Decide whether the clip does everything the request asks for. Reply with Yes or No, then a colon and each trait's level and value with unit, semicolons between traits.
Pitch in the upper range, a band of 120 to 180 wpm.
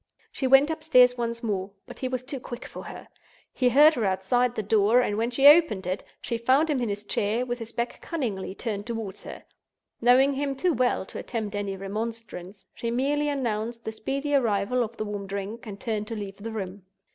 No: high, 230 Hz; fast, 205 wpm